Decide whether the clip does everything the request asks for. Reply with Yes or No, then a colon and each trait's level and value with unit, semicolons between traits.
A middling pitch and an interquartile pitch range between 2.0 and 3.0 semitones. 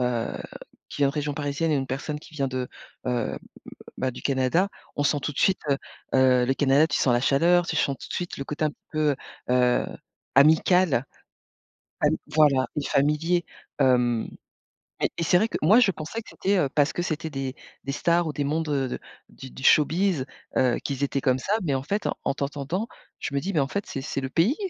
No: medium, 145 Hz; average, 3.6 semitones